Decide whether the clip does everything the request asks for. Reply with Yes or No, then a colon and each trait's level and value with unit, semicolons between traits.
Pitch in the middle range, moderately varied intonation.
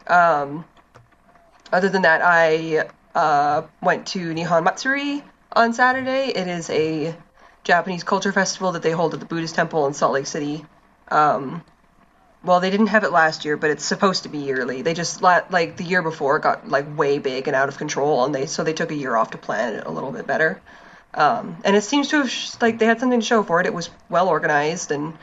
Yes: medium, 170 Hz; average, 4.2 semitones